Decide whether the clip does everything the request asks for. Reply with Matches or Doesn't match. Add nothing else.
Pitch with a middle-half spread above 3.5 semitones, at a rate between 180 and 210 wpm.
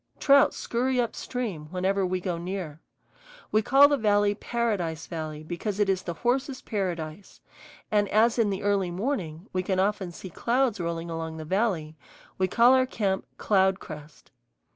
Doesn't match